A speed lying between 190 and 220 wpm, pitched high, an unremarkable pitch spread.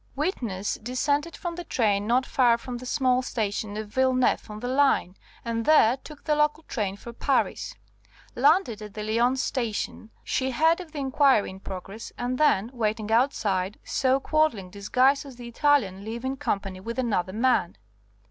No: average, 170 wpm; high, 245 Hz; average, 4.4 semitones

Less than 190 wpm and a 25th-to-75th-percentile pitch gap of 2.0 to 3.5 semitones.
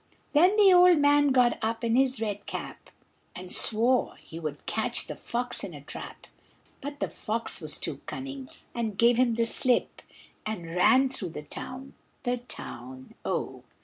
No: average, 170 wpm; average, 4.6 semitones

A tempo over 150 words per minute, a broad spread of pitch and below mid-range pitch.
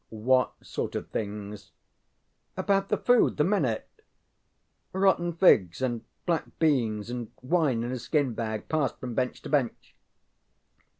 No: average, 145 wpm; wide, 6.5 semitones; low, 130 Hz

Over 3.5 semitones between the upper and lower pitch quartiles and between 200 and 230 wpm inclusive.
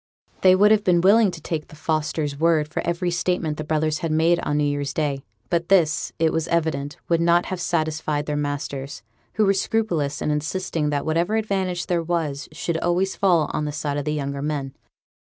No: average, 2.8 semitones; fast, 205 wpm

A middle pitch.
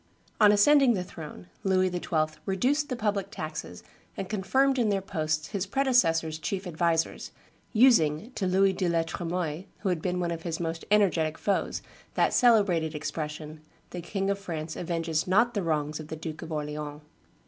Yes: medium, 175 Hz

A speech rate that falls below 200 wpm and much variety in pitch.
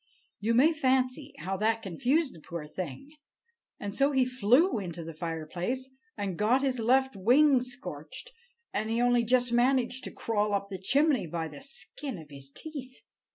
Yes: average, 170 wpm; wide, 6.1 semitones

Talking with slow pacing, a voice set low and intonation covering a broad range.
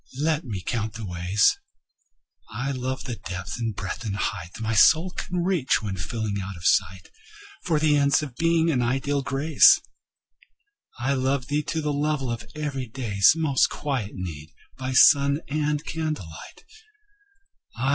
No: average, 155 wpm; low, 130 Hz; wide, 6.2 semitones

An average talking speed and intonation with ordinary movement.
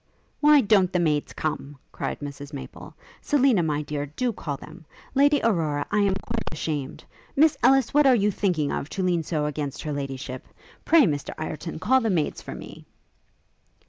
No: average, 175 wpm; wide, 7.6 semitones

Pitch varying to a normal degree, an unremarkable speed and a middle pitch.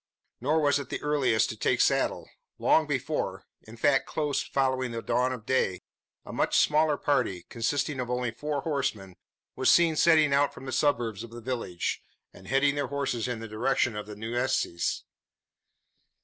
No: average, 4.0 semitones; average, 175 wpm; low, 130 Hz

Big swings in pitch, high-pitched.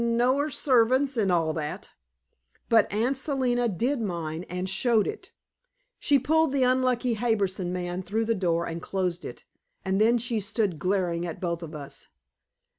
Yes: wide, 5.8 semitones; high, 215 Hz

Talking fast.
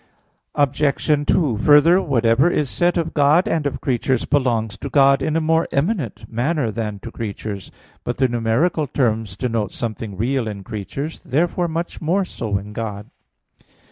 No: average, 160 wpm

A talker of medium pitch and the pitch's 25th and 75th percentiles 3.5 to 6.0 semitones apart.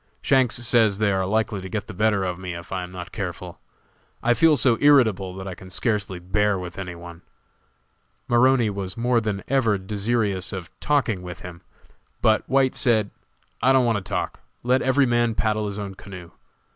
No: low, 105 Hz; average, 4.2 semitones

